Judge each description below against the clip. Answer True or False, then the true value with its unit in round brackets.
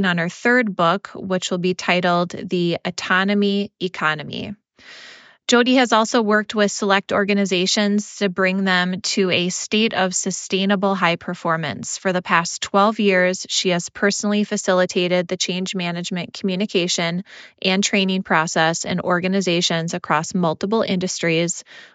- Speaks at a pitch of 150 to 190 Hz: True (185 Hz)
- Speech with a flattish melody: True (2.3 semitones)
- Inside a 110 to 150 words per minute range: True (135 wpm)